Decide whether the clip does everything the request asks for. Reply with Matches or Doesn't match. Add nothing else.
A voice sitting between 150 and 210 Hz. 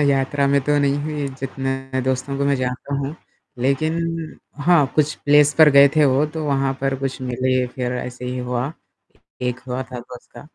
Doesn't match